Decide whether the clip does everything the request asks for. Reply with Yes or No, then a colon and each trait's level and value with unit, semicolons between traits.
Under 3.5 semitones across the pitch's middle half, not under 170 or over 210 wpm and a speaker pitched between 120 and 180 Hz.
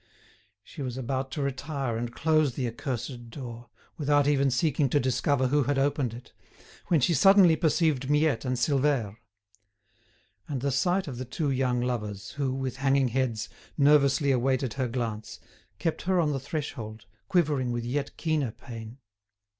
No: average, 3.1 semitones; average, 160 wpm; low, 135 Hz